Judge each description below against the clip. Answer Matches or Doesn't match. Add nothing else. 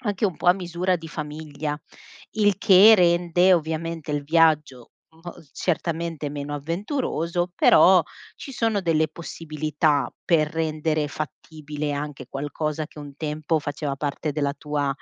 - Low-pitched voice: Doesn't match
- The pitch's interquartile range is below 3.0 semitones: Matches